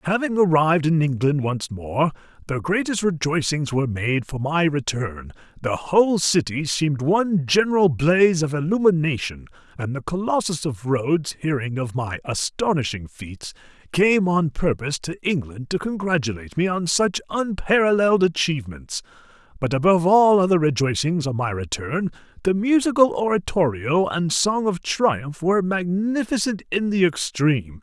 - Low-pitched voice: No, medium, 160 Hz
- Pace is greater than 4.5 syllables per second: Yes, 4.9 syllables/s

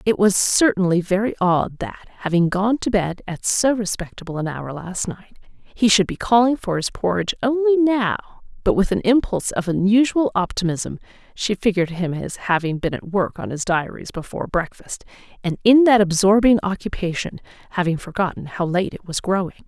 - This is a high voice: Yes, high, 195 Hz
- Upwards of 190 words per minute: No, average, 175 wpm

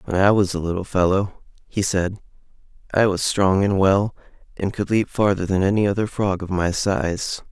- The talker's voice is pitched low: Yes, very low, 95 Hz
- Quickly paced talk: No, average, 190 wpm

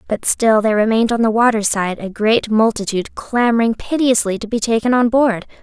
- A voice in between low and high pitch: No, high, 225 Hz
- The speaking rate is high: No, average, 190 wpm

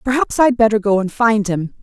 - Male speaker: No, female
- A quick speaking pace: Yes, fast, 230 wpm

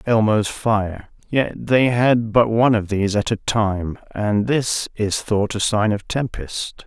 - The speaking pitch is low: Yes, low, 110 Hz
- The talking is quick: No, average, 175 wpm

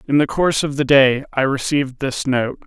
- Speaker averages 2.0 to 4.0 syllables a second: No, 5.4 syllables/s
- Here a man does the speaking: Yes, male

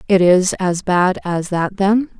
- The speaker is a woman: Yes, female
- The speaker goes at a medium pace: Yes, average, 190 wpm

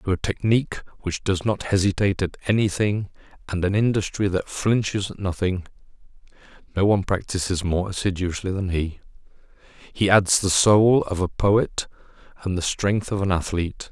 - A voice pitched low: Yes, very low, 95 Hz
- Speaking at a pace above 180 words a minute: No, average, 145 wpm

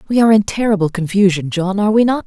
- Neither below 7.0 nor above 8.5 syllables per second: Yes, 7.2 syllables/s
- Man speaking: No, female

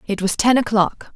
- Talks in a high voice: Yes, high, 215 Hz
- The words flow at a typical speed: No, fast, 210 wpm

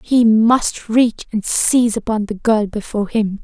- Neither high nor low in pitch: No, high, 220 Hz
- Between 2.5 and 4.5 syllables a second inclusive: Yes, 4.4 syllables/s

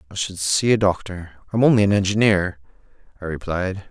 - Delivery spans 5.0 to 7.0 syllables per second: Yes, 5.5 syllables/s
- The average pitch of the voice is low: Yes, very low, 95 Hz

